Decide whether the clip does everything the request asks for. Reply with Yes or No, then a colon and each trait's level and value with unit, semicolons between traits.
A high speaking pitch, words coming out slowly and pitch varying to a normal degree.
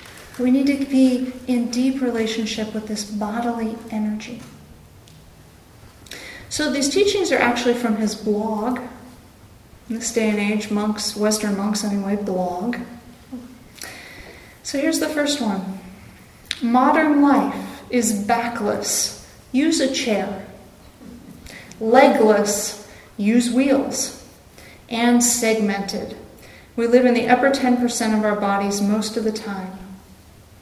Yes: high, 225 Hz; slow, 115 wpm; average, 3.2 semitones